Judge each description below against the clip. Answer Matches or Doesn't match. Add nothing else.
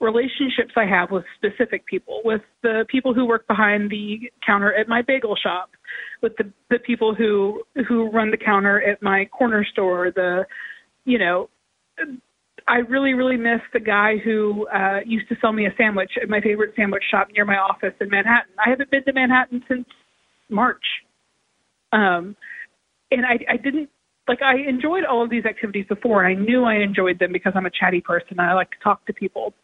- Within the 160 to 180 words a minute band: Doesn't match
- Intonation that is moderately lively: Matches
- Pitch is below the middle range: Doesn't match